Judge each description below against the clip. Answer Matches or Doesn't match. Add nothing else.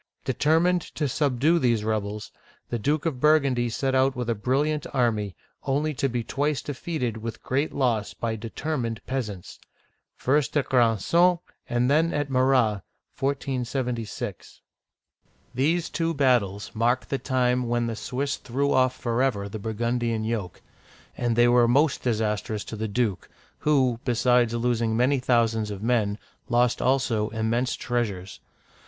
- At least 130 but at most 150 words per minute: Matches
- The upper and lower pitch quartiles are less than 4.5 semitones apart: Matches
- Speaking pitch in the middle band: Doesn't match